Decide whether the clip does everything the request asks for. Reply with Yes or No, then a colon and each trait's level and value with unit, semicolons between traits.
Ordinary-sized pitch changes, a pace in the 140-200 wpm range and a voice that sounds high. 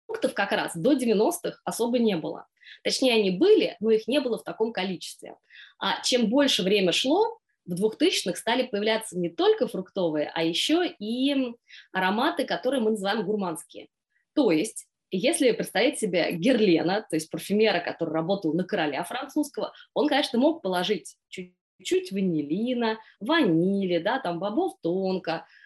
No: wide, 6.6 semitones; average, 145 wpm; high, 215 Hz